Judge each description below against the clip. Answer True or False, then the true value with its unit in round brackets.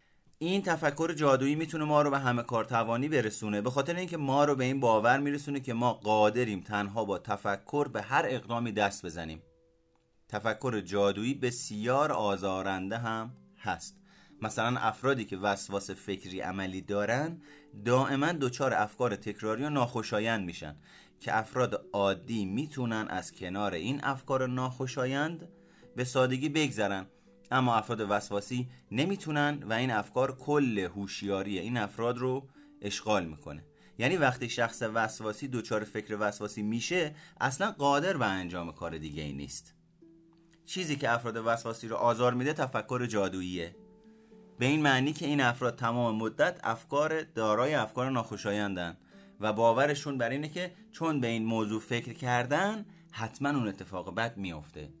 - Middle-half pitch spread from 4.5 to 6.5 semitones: True (5.5 semitones)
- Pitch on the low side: True (120 Hz)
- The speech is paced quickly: False (140 wpm)